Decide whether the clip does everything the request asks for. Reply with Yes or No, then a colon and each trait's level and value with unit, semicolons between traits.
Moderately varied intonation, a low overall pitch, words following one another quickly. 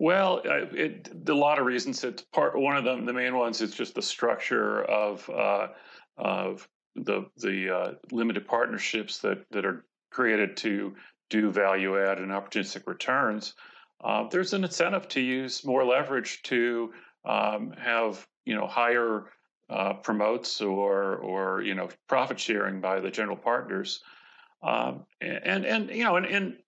No: average, 4.4 semitones; low, 115 Hz; average, 160 wpm